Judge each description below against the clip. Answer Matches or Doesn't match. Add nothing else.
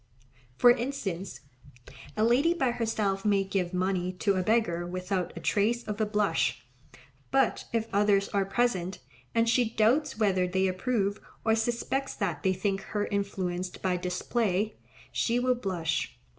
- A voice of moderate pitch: Doesn't match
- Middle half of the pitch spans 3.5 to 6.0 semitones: Matches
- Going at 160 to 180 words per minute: Doesn't match